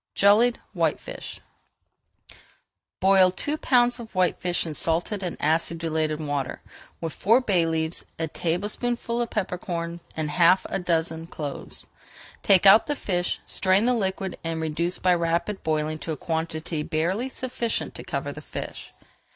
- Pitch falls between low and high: Yes, medium, 175 Hz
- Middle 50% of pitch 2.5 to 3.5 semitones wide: No, average, 4.0 semitones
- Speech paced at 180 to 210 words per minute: No, average, 145 wpm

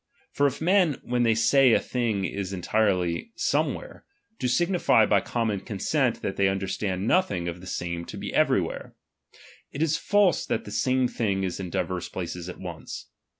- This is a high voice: No, low, 105 Hz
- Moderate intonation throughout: No, wide, 5.8 semitones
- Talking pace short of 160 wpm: No, average, 175 wpm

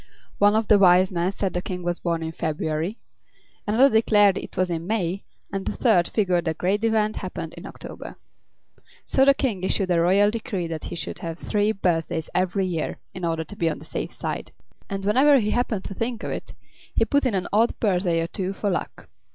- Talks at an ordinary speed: No, fast, 215 wpm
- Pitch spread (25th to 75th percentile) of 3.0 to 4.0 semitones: Yes, average, 3.7 semitones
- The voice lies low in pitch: No, high, 190 Hz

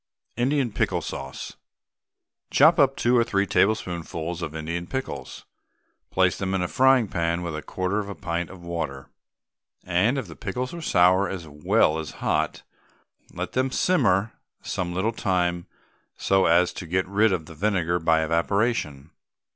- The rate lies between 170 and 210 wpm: No, average, 160 wpm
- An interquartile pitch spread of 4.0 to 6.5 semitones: Yes, average, 4.6 semitones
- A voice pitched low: Yes, very low, 90 Hz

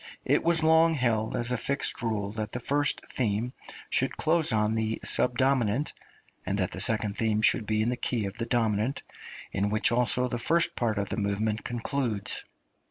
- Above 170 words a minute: Yes, average, 185 wpm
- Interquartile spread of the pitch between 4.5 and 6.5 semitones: No, average, 3.1 semitones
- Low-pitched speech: Yes, low, 115 Hz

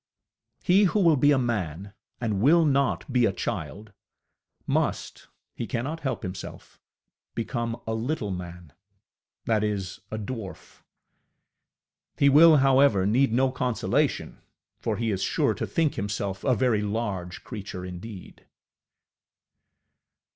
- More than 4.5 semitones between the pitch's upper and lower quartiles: Yes, average, 5.2 semitones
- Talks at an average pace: No, slow, 125 wpm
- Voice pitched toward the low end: Yes, low, 115 Hz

